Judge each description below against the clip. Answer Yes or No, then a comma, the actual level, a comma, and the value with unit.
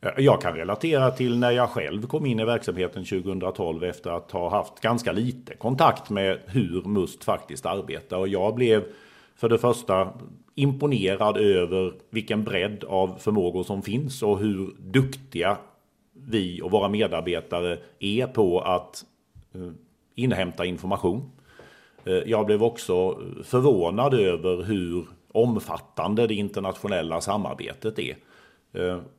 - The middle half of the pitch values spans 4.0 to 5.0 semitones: Yes, average, 4.4 semitones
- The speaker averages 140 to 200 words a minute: No, slow, 125 wpm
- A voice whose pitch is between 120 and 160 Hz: No, low, 105 Hz